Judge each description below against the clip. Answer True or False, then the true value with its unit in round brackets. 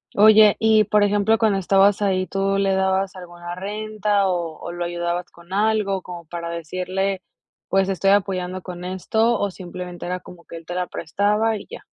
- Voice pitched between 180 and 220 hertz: True (190 Hz)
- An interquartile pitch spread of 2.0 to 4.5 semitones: True (2.5 semitones)